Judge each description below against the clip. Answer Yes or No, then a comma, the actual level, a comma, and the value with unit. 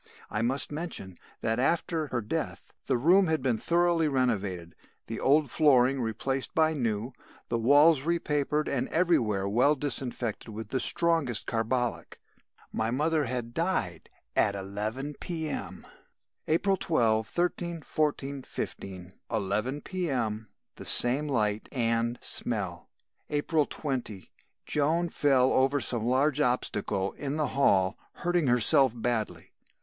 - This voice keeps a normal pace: No, slow, 125 wpm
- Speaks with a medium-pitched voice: No, low, 130 Hz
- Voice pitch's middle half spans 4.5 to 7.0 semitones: Yes, average, 5.2 semitones